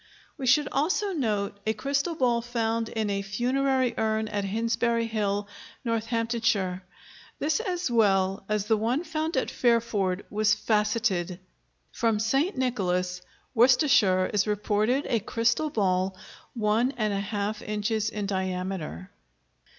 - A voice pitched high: Yes, high, 220 Hz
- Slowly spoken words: Yes, slow, 120 wpm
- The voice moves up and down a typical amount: Yes, average, 3.3 semitones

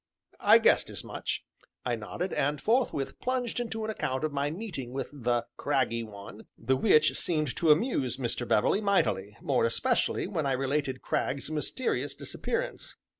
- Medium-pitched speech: Yes, medium, 145 Hz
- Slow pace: No, average, 160 wpm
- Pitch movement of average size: No, wide, 7.8 semitones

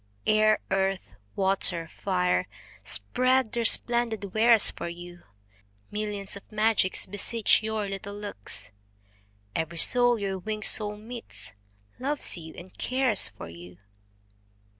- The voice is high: Yes, high, 205 Hz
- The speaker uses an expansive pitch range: No, average, 3.7 semitones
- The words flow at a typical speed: No, slow, 120 wpm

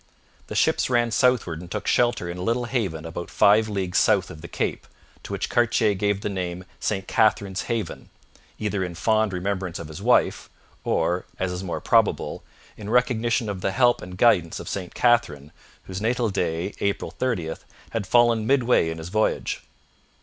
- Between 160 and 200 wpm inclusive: Yes, average, 180 wpm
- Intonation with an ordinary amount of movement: Yes, average, 4.6 semitones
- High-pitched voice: No, low, 100 Hz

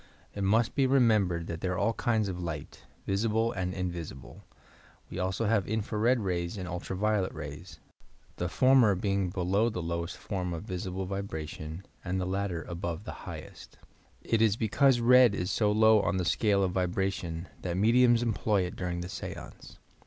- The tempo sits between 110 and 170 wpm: No, average, 180 wpm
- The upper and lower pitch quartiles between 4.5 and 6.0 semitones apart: No, average, 3.6 semitones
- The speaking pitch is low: Yes, very low, 95 Hz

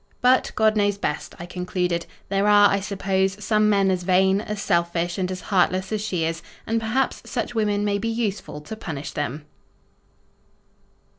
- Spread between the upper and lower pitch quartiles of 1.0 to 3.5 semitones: Yes, average, 2.9 semitones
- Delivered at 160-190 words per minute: Yes, average, 170 wpm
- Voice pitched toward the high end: Yes, high, 195 Hz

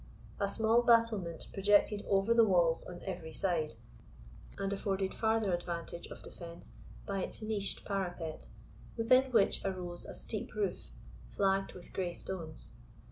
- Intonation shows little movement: No, average, 3.6 semitones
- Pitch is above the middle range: Yes, high, 195 Hz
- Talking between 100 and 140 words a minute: Yes, slow, 135 wpm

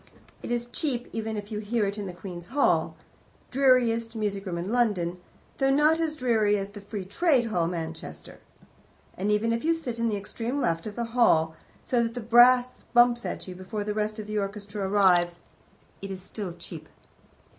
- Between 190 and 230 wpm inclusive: Yes, average, 195 wpm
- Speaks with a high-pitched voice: Yes, high, 215 Hz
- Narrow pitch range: No, average, 3.6 semitones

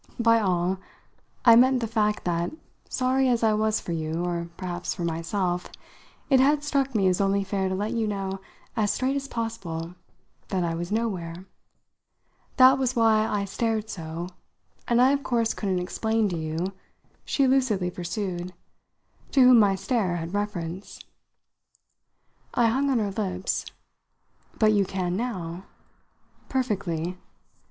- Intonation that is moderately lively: Yes, average, 4.6 semitones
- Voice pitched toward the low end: No, high, 200 Hz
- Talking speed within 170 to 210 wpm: No, average, 150 wpm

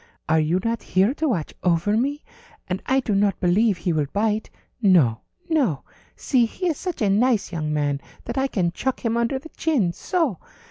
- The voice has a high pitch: Yes, high, 210 Hz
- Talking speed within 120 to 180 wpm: No, average, 195 wpm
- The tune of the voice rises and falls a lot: Yes, wide, 7.2 semitones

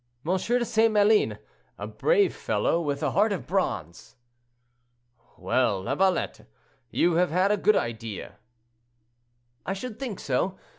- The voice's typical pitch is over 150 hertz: Yes, high, 190 Hz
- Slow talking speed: Yes, slow, 130 wpm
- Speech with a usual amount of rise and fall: No, wide, 6.8 semitones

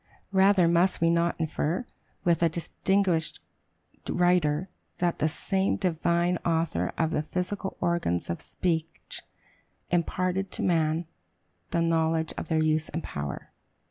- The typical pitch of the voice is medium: Yes, medium, 170 Hz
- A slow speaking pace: Yes, slow, 130 wpm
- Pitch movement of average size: No, narrow, 2.0 semitones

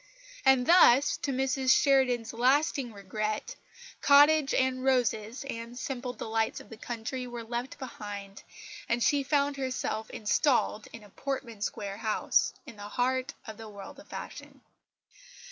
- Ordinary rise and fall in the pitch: Yes, average, 3.4 semitones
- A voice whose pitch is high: Yes, high, 245 Hz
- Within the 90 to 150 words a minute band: Yes, average, 145 wpm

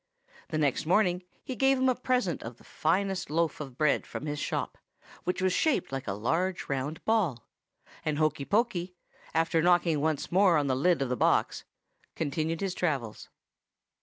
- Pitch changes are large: No, average, 4.5 semitones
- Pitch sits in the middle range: Yes, medium, 165 Hz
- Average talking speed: Yes, average, 175 wpm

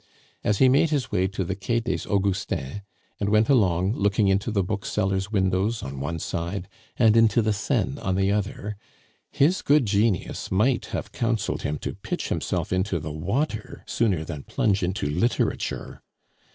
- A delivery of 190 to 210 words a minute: No, average, 165 wpm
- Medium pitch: No, low, 100 Hz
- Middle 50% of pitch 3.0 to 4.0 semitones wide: Yes, average, 3.3 semitones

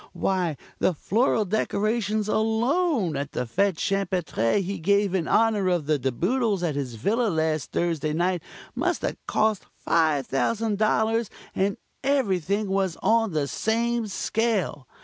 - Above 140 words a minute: No, slow, 135 wpm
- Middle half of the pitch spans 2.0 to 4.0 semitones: No, wide, 5.5 semitones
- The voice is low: No, high, 195 Hz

